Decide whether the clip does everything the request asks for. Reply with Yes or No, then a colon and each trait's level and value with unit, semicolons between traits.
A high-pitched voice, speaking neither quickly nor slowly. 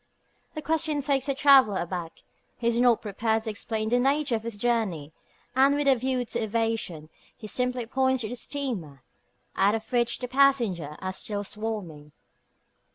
Yes: high, 230 Hz; average, 170 wpm